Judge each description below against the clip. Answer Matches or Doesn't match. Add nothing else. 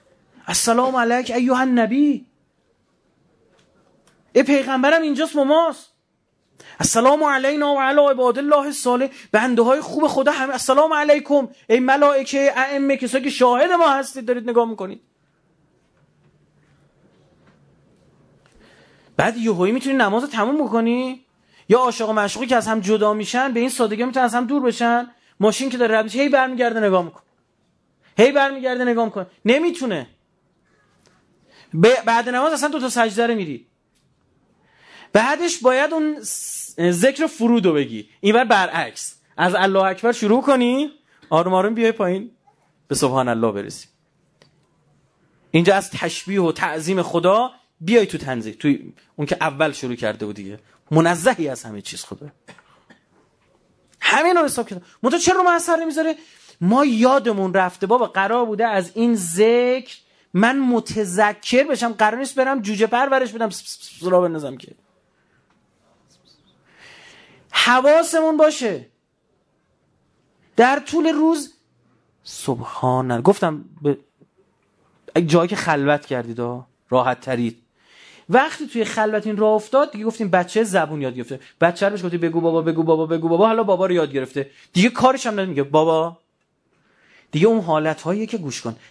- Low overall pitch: Doesn't match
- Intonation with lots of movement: Matches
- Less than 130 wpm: Doesn't match